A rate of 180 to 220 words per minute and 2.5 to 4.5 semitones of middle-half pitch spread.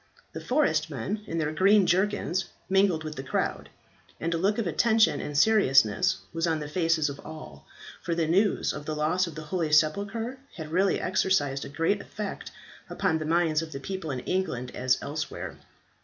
Yes: average, 185 wpm; average, 4.0 semitones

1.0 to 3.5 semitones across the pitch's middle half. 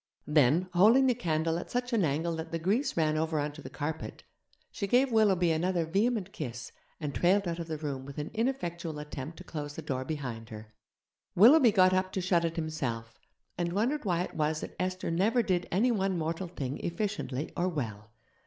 No: average, 4.5 semitones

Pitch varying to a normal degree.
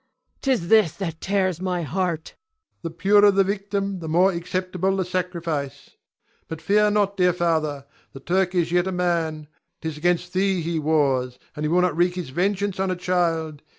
Yes: average, 3.0 semitones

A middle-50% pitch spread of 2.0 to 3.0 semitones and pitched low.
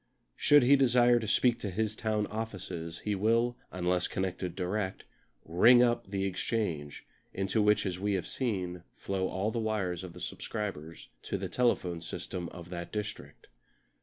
No: average, 3.8 semitones; low, 100 Hz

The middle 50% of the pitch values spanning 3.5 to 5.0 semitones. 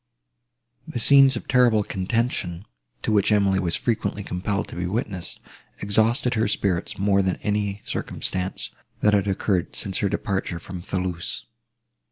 No: average, 2.7 semitones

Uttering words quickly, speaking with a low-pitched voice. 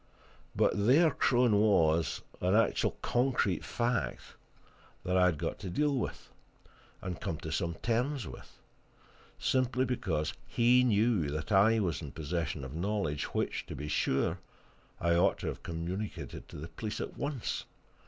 No: average, 155 wpm; very low, 95 Hz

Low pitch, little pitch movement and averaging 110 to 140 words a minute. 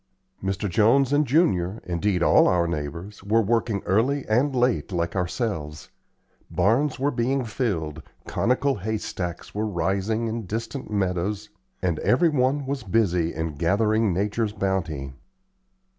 No: low, 105 Hz; average, 5.1 semitones; slow, 135 wpm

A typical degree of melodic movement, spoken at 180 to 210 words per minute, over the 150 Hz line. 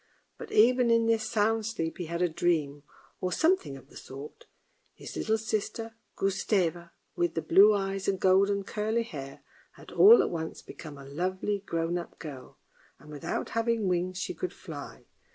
No: average, 5.0 semitones; average, 170 wpm; high, 190 Hz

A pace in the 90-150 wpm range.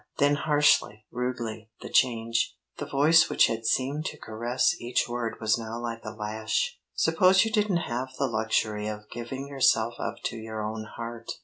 No: average, 175 wpm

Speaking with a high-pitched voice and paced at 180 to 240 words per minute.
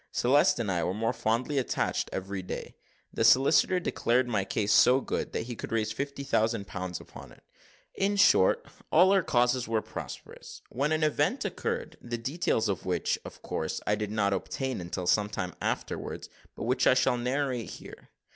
No: low, 120 Hz; average, 185 wpm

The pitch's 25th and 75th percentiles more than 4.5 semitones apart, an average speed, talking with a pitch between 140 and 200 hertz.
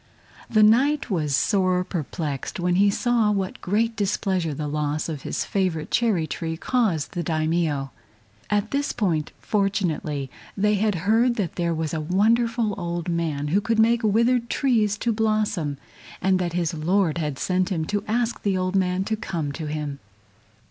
Yes: average, 5.1 semitones; average, 170 wpm; medium, 185 Hz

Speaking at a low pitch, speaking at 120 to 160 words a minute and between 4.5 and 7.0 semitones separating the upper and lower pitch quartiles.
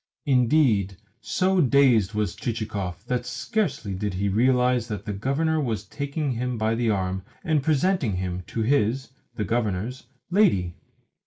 Yes: low, 115 Hz; average, 145 wpm; wide, 5.4 semitones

